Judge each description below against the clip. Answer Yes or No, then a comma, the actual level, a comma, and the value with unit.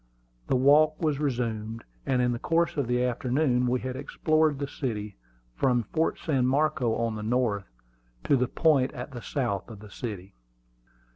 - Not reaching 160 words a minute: No, average, 170 wpm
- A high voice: No, low, 125 Hz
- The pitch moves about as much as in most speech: Yes, average, 3.7 semitones